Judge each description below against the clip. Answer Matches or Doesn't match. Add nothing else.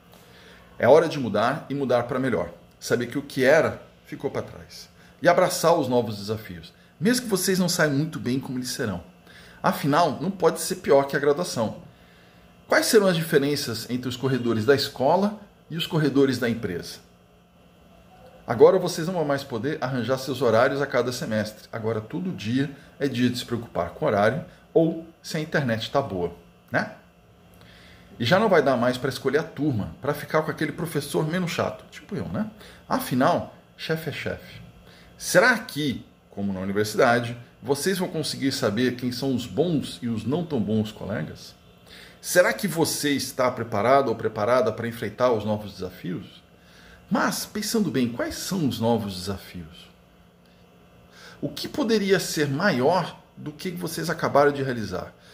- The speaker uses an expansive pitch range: Matches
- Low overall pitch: Matches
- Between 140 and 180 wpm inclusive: Matches